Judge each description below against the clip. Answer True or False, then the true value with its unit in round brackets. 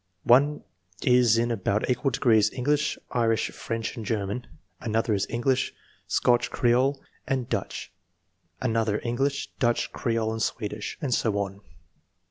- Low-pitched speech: True (120 Hz)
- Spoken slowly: True (130 wpm)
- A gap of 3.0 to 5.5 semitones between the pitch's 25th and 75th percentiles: False (2.4 semitones)